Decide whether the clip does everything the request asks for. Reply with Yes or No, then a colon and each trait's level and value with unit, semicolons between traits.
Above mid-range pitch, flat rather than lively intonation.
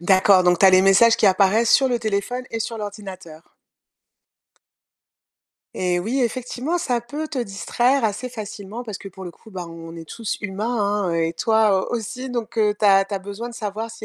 No: high, 210 Hz; average, 3.6 semitones